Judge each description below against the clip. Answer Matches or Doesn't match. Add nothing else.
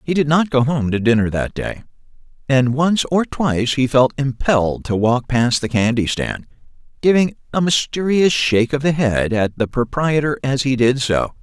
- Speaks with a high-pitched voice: Doesn't match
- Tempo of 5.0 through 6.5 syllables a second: Doesn't match